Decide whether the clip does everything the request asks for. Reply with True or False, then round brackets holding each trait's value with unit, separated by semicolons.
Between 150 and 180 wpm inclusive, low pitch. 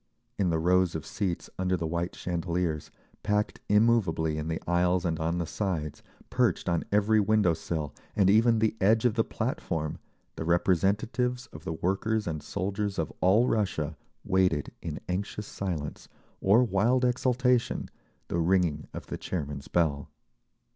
True (155 wpm; 90 Hz)